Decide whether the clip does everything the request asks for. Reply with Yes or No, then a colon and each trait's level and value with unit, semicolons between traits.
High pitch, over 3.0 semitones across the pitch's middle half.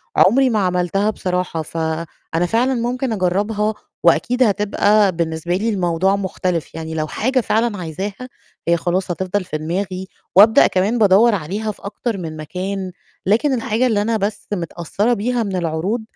Yes: high, 195 Hz; average, 3.9 semitones